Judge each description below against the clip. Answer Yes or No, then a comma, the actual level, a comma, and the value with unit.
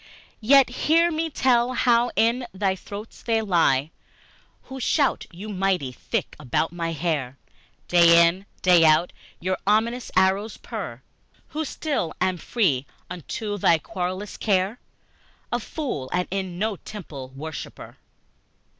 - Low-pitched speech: No, high, 190 Hz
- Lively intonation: Yes, wide, 5.7 semitones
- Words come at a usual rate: No, slow, 130 wpm